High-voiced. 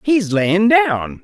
No: medium, 175 Hz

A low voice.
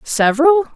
No: very high, 300 Hz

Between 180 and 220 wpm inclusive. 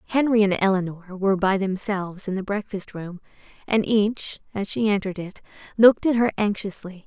No: average, 170 wpm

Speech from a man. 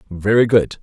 Yes: male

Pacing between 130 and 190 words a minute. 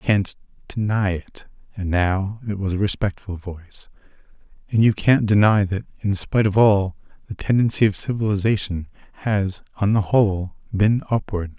Yes: average, 150 wpm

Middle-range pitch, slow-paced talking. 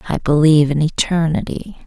Yes: medium, 155 Hz; slow, 130 wpm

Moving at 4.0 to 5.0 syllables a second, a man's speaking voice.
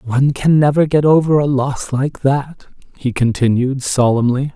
Yes: 4.5 syllables/s; male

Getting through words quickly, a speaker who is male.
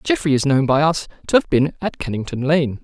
Yes: fast, 235 wpm; male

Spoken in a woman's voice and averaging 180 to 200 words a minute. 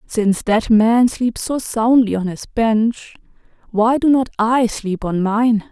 No: female; average, 170 wpm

